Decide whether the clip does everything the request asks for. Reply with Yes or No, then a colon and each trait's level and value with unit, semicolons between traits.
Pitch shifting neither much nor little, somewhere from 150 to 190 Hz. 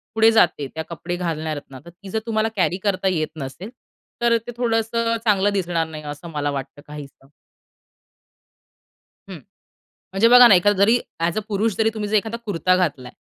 No: wide, 5.8 semitones; medium, 185 Hz